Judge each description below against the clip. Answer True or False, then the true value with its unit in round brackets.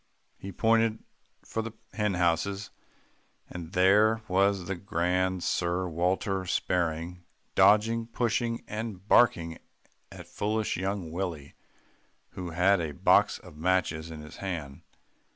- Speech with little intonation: False (3.6 semitones)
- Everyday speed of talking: False (120 wpm)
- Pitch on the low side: True (95 Hz)